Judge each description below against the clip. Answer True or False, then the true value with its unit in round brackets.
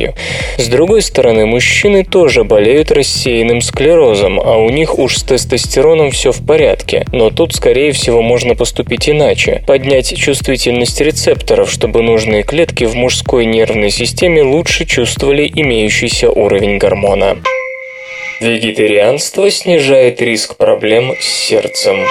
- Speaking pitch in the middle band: True (155 Hz)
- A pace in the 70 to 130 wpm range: True (120 wpm)